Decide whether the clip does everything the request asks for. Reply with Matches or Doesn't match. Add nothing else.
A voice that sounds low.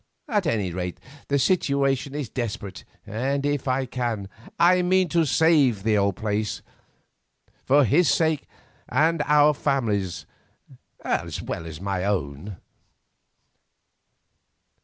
Matches